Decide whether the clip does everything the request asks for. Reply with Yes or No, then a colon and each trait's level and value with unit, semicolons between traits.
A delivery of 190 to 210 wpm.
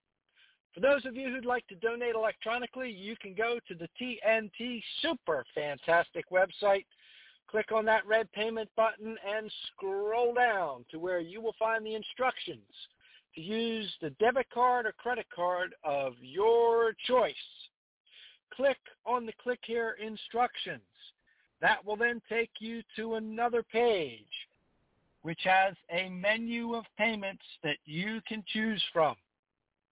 No: average, 140 wpm